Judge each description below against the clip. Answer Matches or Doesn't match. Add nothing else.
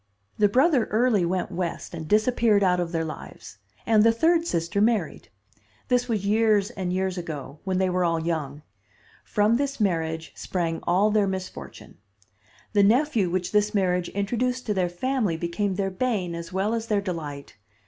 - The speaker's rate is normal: Matches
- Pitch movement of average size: Matches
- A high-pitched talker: Matches